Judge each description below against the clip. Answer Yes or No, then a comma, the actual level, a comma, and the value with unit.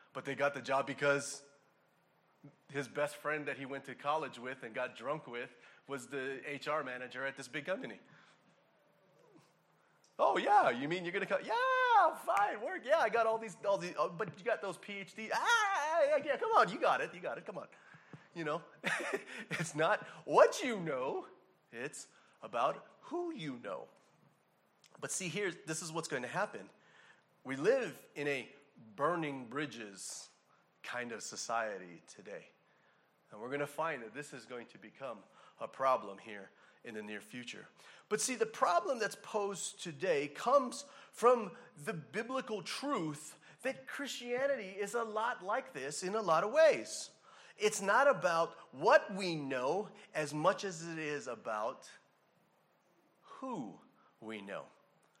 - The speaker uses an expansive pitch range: Yes, wide, 8.4 semitones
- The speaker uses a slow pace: No, average, 160 wpm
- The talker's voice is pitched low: No, medium, 175 Hz